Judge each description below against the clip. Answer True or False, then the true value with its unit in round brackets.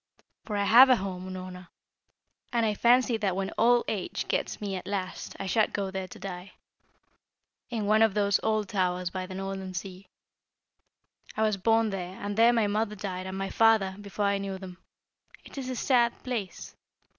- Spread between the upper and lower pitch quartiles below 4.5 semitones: True (2.8 semitones)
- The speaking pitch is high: True (200 Hz)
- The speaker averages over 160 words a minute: True (190 wpm)